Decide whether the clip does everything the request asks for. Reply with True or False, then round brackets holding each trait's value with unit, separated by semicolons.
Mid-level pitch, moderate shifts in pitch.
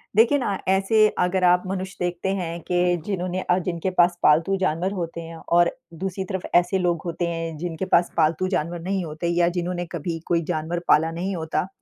False (175 Hz; 1.9 semitones)